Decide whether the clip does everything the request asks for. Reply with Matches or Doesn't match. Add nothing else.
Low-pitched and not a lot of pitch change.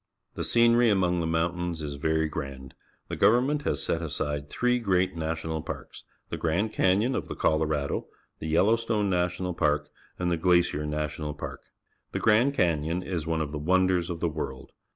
Doesn't match